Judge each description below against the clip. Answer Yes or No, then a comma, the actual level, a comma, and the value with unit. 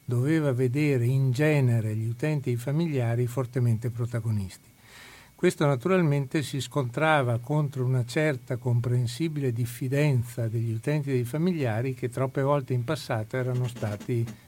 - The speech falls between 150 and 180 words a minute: No, average, 135 wpm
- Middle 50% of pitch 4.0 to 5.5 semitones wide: No, average, 3.2 semitones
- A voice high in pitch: No, low, 130 Hz